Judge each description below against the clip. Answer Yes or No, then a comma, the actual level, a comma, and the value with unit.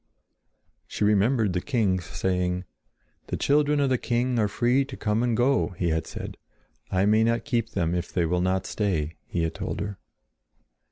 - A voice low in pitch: Yes, low, 105 Hz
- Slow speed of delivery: No, average, 180 wpm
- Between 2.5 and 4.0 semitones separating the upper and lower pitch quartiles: No, average, 5.1 semitones